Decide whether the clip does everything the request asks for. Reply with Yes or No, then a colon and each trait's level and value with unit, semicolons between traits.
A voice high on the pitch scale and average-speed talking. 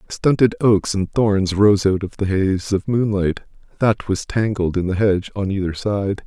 No: low, 100 Hz; average, 190 wpm